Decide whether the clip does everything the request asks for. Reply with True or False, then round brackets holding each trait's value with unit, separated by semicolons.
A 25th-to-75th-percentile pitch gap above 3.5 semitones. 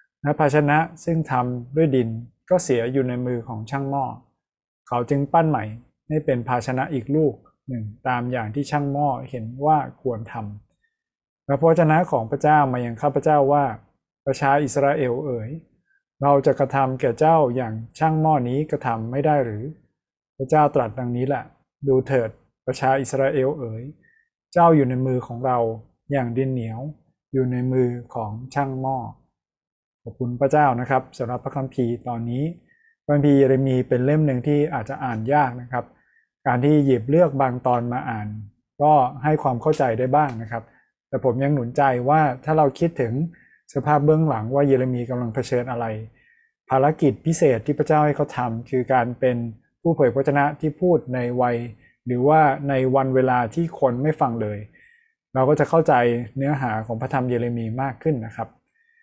False (3.2 semitones)